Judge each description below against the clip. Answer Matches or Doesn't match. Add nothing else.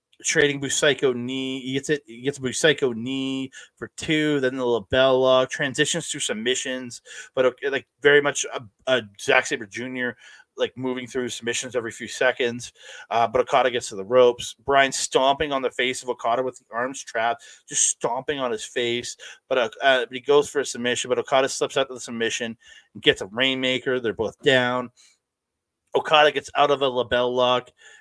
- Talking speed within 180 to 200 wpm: Matches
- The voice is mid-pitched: Doesn't match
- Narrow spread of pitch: Matches